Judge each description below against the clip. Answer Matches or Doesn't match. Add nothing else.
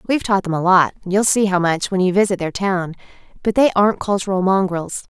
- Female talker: Matches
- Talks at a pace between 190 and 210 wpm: Matches